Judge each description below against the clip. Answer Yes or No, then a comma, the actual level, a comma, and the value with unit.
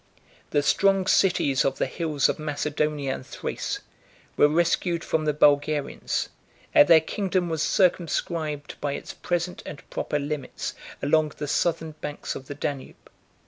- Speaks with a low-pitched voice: No, medium, 150 Hz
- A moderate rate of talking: Yes, average, 145 wpm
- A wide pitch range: No, average, 2.8 semitones